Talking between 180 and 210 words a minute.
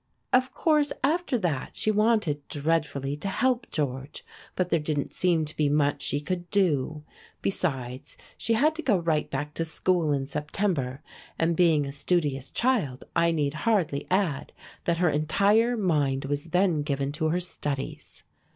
No: average, 160 wpm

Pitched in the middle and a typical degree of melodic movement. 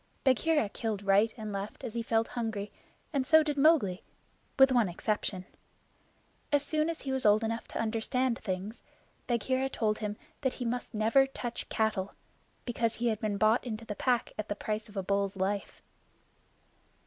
No: high, 225 Hz; average, 3.6 semitones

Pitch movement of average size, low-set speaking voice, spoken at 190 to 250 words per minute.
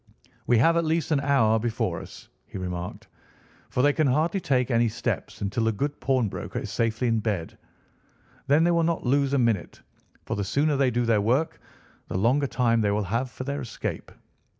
Yes: average, 4.1 semitones; low, 125 Hz; average, 195 wpm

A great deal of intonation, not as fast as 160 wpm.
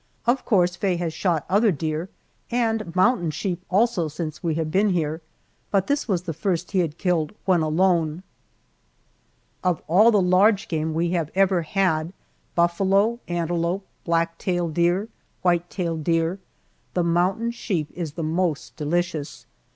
No: average, 2.8 semitones; average, 150 wpm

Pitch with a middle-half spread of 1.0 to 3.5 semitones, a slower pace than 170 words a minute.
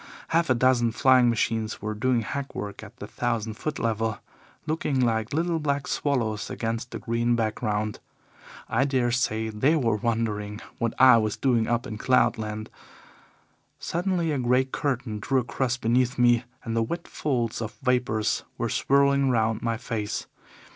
Yes: average, 2.9 semitones; average, 160 wpm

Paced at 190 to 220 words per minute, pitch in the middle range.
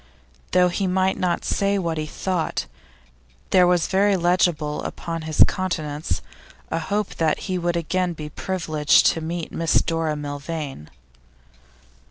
No: average, 140 wpm; medium, 170 Hz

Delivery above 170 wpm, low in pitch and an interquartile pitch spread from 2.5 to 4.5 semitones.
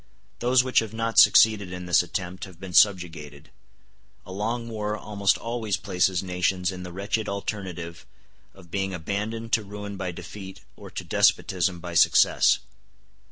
No: average, 155 wpm; very low, 95 Hz; average, 2.9 semitones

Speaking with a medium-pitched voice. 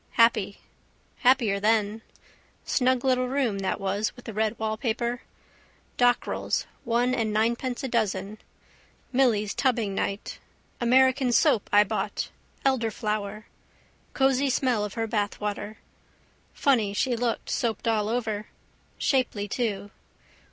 No: high, 225 Hz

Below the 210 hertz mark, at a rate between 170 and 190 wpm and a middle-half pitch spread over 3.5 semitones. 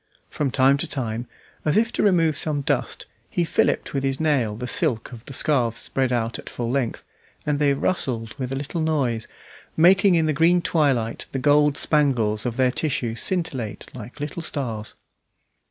Yes: low, 135 Hz; average, 180 wpm; average, 4.4 semitones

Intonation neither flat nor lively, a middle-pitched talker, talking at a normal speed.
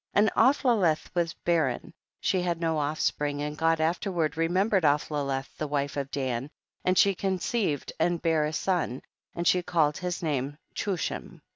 Yes: average, 3.4 semitones; medium, 165 Hz; average, 165 wpm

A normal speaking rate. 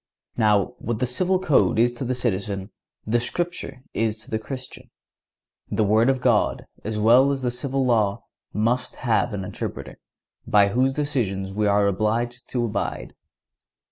Yes: average, 160 wpm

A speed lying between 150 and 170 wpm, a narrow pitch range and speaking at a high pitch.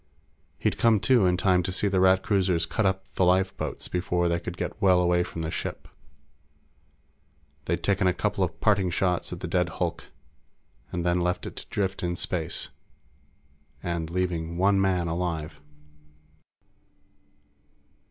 No: average, 155 wpm; narrow, 1.6 semitones; very low, 90 Hz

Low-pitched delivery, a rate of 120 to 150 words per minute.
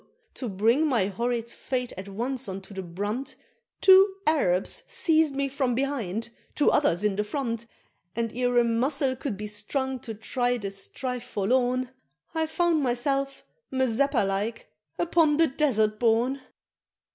No: high, 245 Hz; average, 145 wpm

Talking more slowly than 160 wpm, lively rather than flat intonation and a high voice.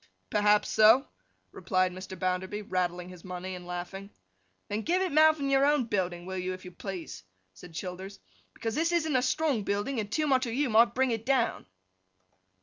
No: average, 190 wpm; wide, 6.2 semitones; high, 205 Hz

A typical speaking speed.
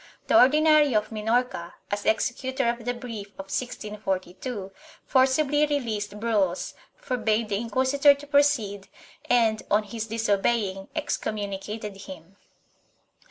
No: slow, 115 wpm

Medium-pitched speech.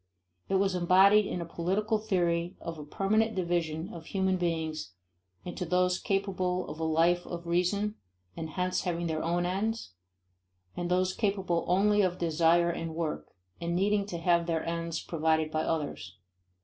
Yes: medium, 175 Hz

